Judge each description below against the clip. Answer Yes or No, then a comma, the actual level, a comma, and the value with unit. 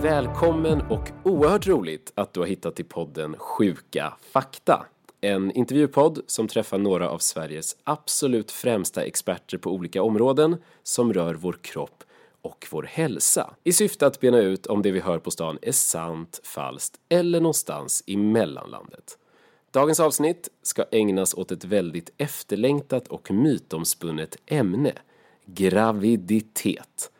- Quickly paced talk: No, average, 135 wpm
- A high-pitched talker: No, low, 115 Hz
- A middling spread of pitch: No, wide, 8.7 semitones